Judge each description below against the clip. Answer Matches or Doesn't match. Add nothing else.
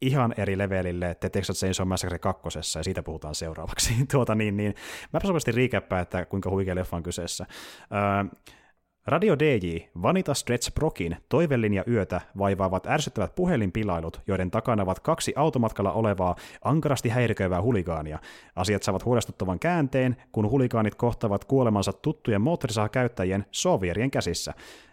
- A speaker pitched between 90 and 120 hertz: Matches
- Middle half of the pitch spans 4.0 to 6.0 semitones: Matches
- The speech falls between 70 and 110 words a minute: Doesn't match